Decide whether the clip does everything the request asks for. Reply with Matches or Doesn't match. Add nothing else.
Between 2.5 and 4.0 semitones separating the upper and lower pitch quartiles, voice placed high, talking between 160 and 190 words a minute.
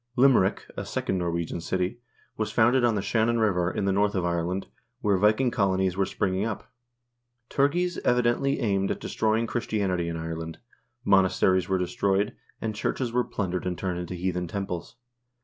Doesn't match